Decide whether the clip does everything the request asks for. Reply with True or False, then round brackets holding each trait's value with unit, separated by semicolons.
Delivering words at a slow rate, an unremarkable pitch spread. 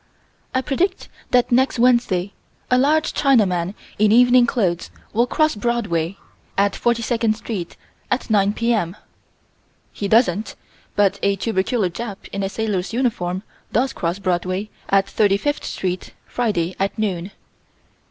True (130 wpm; 4.1 semitones)